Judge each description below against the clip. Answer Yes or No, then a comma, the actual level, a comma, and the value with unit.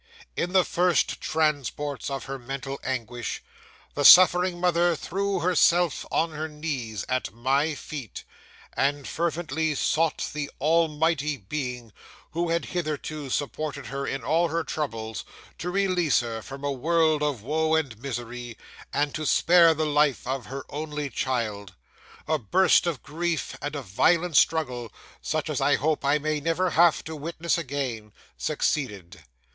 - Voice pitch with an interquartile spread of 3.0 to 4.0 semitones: Yes, average, 3.7 semitones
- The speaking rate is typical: Yes, average, 150 wpm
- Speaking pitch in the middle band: Yes, medium, 150 Hz